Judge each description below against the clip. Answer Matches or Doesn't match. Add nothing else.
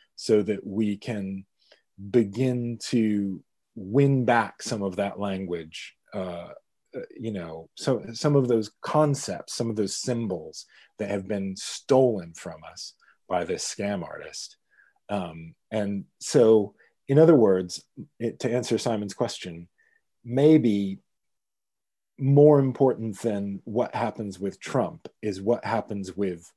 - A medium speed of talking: Doesn't match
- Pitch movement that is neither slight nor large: Matches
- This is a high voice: Doesn't match